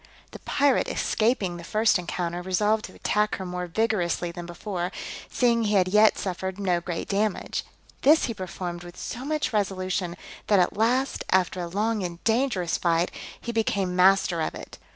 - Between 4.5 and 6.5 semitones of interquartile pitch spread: No, average, 3.7 semitones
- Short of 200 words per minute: Yes, average, 175 wpm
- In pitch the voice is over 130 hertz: Yes, high, 190 Hz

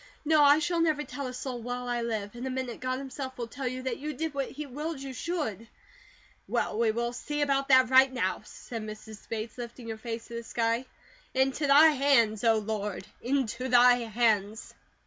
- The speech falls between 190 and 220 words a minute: Yes, fast, 205 wpm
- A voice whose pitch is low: No, very high, 250 Hz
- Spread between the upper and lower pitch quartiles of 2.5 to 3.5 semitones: Yes, average, 3.2 semitones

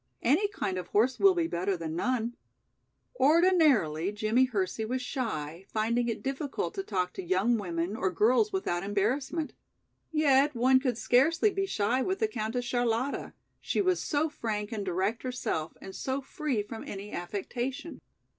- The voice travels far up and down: Yes, wide, 6.0 semitones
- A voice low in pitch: No, high, 240 Hz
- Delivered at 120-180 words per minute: Yes, average, 160 wpm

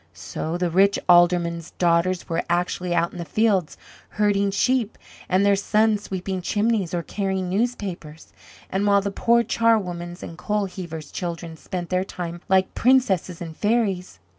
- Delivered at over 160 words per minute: No, average, 155 wpm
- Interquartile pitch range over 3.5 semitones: No, average, 2.9 semitones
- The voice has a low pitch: No, medium, 185 Hz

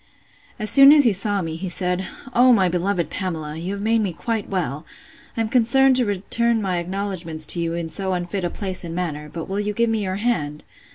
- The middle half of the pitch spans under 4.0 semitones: No, average, 4.3 semitones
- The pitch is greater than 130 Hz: Yes, high, 190 Hz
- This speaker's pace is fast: Yes, fast, 220 wpm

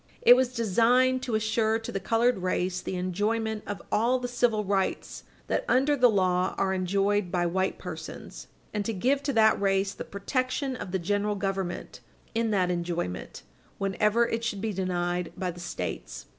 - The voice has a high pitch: Yes, high, 205 Hz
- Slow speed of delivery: No, average, 175 wpm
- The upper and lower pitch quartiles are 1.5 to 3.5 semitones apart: No, average, 3.9 semitones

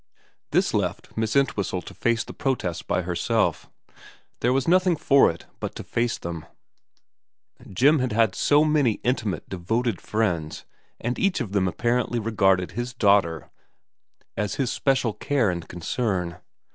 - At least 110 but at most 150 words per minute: Yes, average, 145 wpm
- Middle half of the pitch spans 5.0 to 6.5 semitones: Yes, wide, 5.6 semitones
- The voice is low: Yes, low, 115 Hz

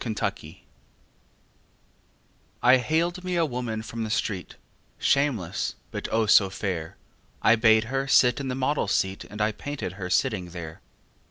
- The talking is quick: No, average, 155 wpm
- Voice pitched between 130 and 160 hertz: No, low, 110 Hz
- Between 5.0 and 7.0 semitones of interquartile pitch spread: Yes, wide, 5.5 semitones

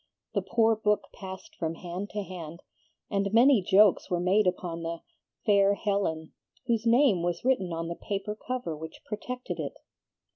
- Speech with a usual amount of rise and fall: Yes, average, 4.1 semitones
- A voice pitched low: No, high, 195 Hz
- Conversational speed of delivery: Yes, average, 160 wpm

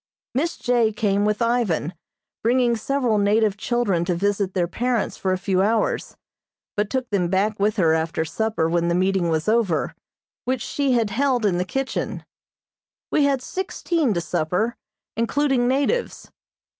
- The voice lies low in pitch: No, high, 215 Hz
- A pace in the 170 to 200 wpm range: No, average, 155 wpm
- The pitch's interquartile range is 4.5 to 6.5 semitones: Yes, average, 5.0 semitones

